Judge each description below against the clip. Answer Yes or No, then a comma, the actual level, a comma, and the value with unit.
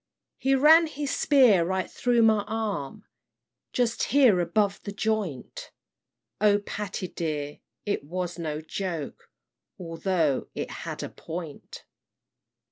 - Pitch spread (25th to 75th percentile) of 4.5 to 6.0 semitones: Yes, average, 5.1 semitones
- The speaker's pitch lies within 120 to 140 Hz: No, high, 200 Hz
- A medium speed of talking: No, slow, 120 wpm